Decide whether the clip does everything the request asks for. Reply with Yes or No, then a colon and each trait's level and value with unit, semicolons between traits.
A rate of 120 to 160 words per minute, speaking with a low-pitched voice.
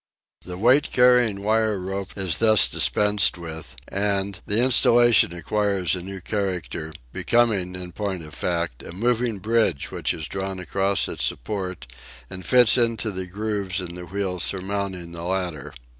Yes: average, 155 wpm; very low, 95 Hz